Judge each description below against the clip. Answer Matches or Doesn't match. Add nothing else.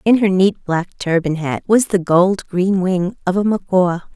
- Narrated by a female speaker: Matches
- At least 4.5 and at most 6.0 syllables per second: Doesn't match